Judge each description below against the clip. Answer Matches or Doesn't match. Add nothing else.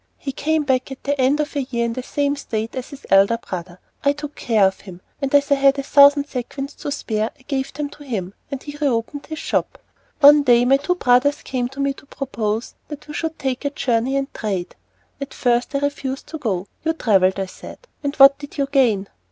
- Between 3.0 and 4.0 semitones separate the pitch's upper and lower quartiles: Matches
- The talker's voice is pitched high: Matches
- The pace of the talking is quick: Matches